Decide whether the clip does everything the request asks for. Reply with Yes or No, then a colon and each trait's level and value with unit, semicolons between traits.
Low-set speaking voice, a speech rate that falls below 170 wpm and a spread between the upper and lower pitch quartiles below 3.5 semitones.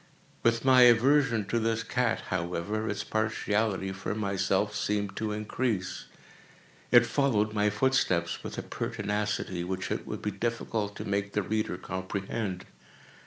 Yes: low, 105 Hz; average, 140 wpm; narrow, 2.6 semitones